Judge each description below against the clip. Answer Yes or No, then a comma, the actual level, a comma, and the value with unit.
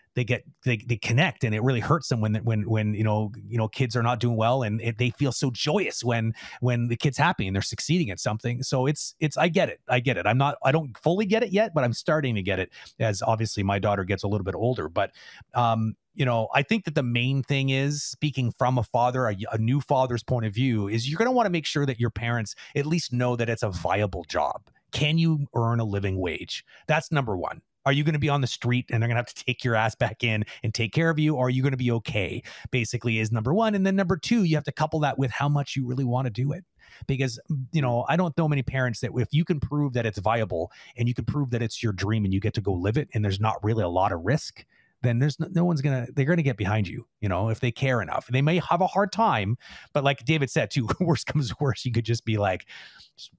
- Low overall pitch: Yes, low, 125 Hz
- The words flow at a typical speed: No, fast, 280 wpm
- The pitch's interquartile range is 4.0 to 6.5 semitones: Yes, average, 4.4 semitones